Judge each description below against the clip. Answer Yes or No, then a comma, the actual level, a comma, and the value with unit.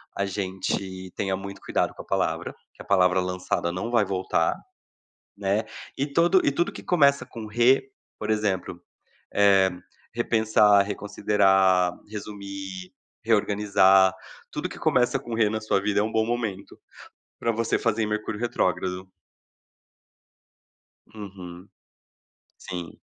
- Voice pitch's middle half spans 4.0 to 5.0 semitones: No, average, 2.7 semitones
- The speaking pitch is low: Yes, low, 100 Hz